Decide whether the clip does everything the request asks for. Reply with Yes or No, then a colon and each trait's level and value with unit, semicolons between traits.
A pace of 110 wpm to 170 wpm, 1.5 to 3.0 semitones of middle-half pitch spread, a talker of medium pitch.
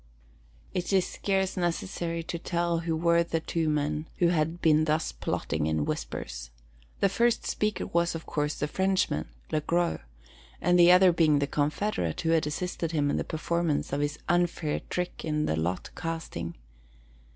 Yes: average, 165 wpm; average, 2.7 semitones; medium, 165 Hz